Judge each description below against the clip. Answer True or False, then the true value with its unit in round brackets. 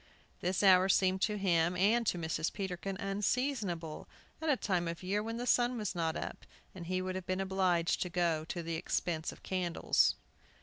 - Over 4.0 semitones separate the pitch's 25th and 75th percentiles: False (2.6 semitones)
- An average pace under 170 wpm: False (190 wpm)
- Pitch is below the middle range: False (185 Hz)